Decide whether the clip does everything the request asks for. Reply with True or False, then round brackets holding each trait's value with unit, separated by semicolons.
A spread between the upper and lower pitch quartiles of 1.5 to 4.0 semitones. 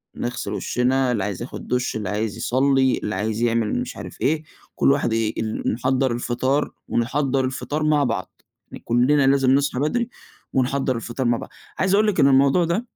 True (3.1 semitones)